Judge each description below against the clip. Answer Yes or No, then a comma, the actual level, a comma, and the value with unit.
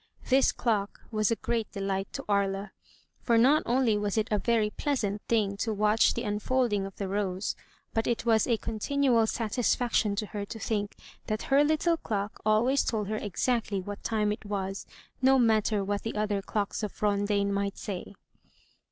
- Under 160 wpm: No, average, 180 wpm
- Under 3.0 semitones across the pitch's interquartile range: Yes, narrow, 2.5 semitones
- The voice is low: No, high, 215 Hz